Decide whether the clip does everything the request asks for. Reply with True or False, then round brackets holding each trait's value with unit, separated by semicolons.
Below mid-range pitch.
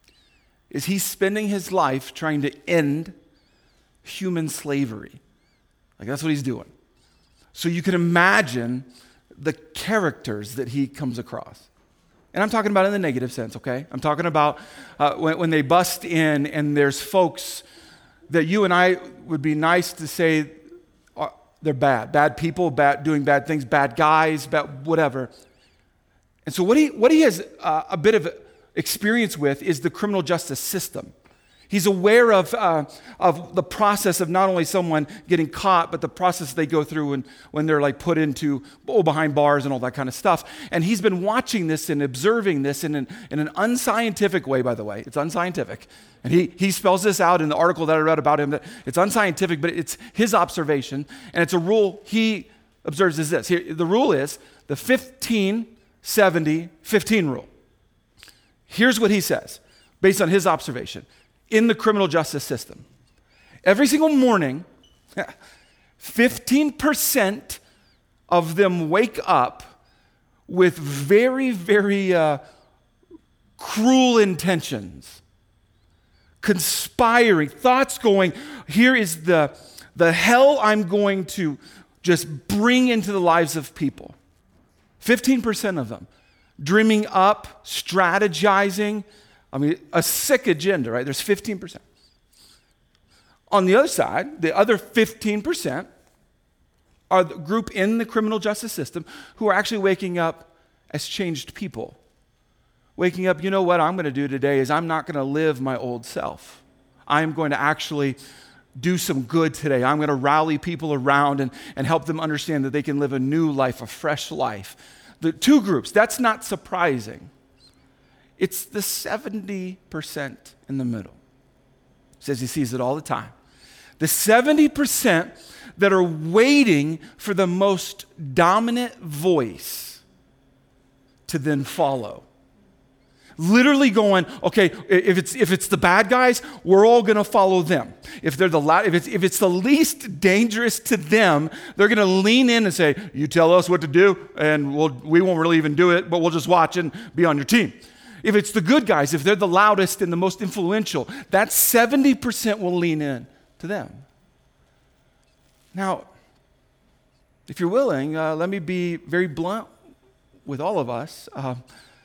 False (175 Hz)